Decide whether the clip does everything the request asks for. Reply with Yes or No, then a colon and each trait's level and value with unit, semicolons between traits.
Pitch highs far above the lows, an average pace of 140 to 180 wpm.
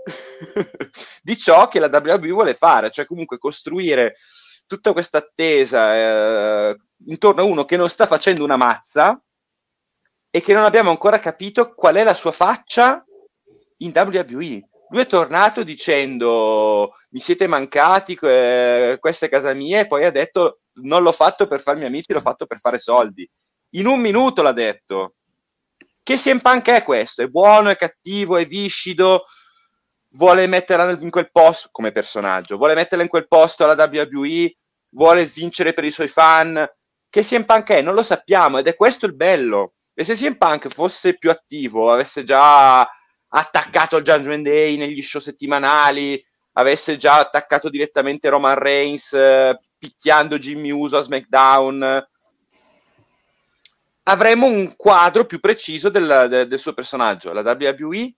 Yes: wide, 6.7 semitones; average, 155 wpm